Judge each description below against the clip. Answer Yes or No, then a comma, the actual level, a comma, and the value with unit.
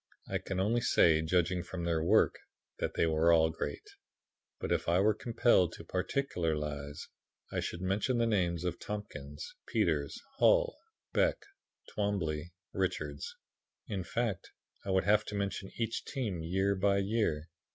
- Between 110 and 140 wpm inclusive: No, average, 150 wpm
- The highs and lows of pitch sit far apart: No, average, 4.4 semitones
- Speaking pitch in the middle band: No, very low, 95 Hz